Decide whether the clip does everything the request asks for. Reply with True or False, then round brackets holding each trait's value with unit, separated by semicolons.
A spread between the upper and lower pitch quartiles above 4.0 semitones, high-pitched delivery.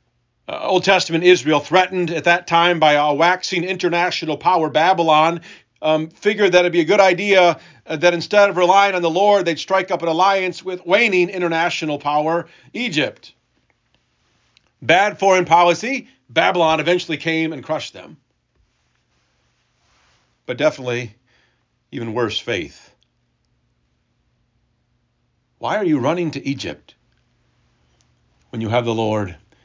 False (4.7 semitones; 165 Hz)